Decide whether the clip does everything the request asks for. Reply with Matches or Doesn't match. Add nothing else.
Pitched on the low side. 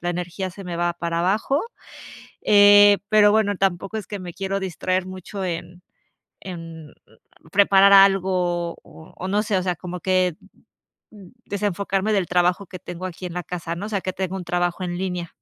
Doesn't match